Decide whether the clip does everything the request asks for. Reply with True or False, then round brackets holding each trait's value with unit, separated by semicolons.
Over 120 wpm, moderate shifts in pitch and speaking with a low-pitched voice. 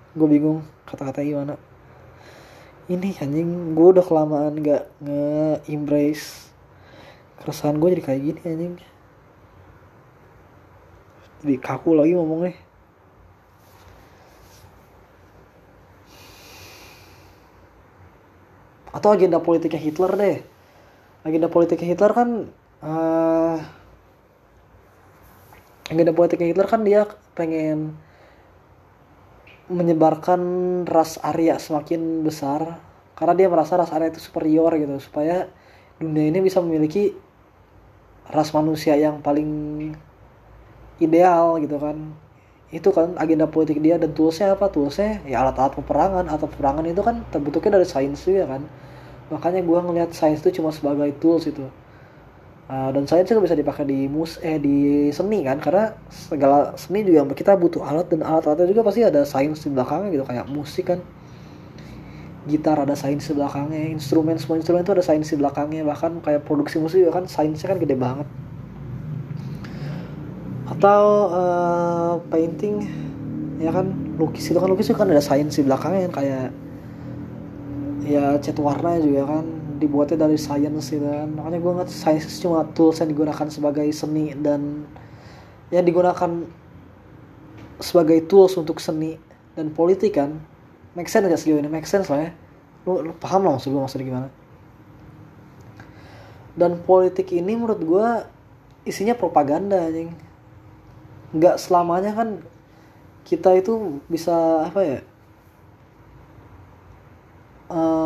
False (130 wpm; 3.4 semitones; 155 Hz)